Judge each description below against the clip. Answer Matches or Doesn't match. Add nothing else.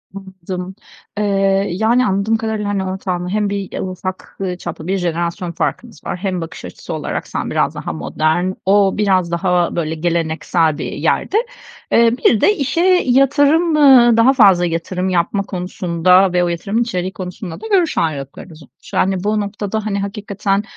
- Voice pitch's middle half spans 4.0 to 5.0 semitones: Doesn't match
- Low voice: Doesn't match